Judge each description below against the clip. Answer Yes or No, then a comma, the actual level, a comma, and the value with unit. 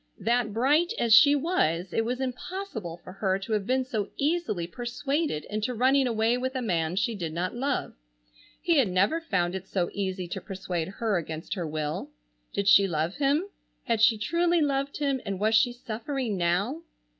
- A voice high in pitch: Yes, high, 220 Hz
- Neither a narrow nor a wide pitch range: No, wide, 6.3 semitones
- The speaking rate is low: No, average, 185 wpm